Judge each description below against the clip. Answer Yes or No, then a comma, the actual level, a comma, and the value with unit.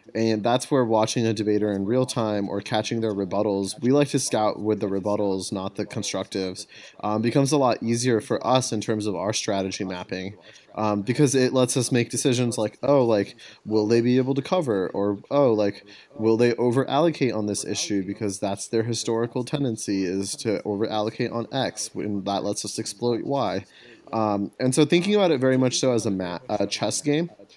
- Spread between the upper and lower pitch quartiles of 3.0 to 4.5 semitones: Yes, average, 3.7 semitones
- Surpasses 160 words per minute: Yes, average, 200 wpm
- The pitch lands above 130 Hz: No, low, 110 Hz